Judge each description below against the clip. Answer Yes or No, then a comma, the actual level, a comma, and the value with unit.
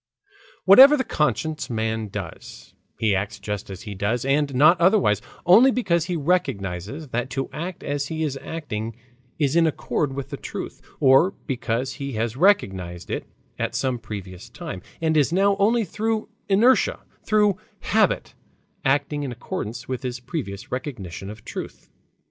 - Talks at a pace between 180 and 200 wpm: No, average, 155 wpm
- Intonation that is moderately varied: No, wide, 7.5 semitones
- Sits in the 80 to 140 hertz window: Yes, low, 135 Hz